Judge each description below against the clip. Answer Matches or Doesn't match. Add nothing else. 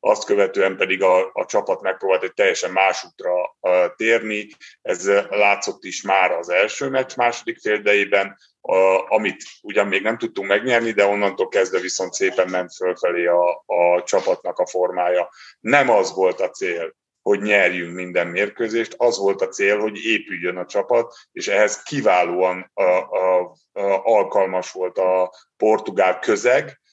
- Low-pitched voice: Matches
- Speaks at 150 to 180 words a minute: Matches